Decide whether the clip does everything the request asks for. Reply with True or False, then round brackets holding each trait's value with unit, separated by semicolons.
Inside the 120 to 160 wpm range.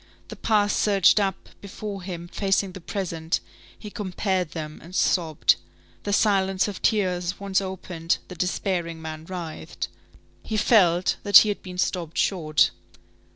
True (145 wpm)